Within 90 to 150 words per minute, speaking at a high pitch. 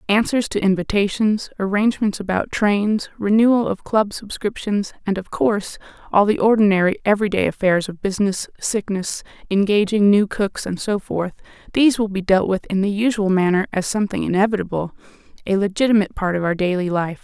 No: average, 160 wpm; high, 200 Hz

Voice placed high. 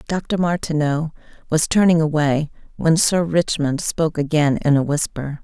No: medium, 155 Hz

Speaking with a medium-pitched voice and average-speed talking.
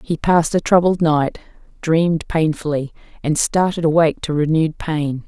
Yes: medium, 160 Hz; average, 150 wpm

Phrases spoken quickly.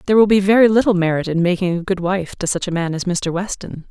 Yes: fast, 275 wpm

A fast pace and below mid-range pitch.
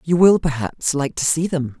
No: fast, 235 wpm; medium, 150 Hz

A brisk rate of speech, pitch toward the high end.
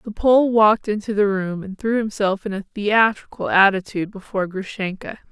No: average, 170 wpm; high, 205 Hz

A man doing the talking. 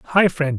Yes: male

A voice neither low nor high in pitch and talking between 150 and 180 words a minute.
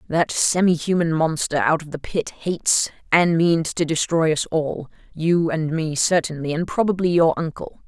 Yes: medium, 165 Hz; average, 170 wpm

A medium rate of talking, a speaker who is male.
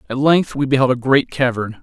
No: fast, 230 wpm; male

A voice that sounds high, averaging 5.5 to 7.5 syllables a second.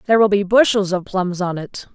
Yes: high, 195 Hz; 5.7 syllables/s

